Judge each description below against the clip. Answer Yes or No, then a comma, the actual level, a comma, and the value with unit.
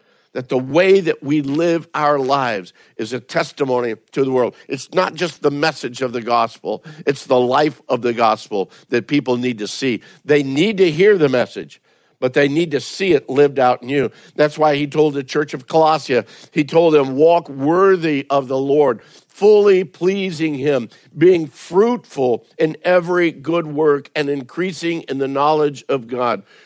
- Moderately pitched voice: Yes, medium, 150 Hz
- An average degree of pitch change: Yes, average, 3.7 semitones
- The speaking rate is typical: Yes, average, 180 wpm